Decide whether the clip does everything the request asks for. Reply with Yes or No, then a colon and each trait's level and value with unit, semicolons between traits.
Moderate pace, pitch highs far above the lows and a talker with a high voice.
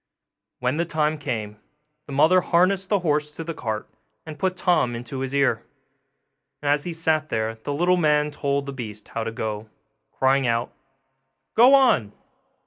No: average, 170 wpm; wide, 5.8 semitones; medium, 145 Hz